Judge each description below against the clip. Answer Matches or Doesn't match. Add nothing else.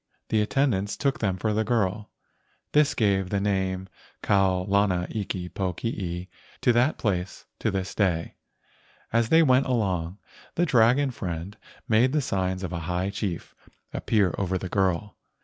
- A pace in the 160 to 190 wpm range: Doesn't match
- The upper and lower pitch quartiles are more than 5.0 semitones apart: Doesn't match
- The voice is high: Doesn't match